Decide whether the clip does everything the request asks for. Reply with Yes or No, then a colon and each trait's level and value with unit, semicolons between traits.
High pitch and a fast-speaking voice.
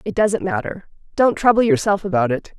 No: high, 210 Hz; average, 185 wpm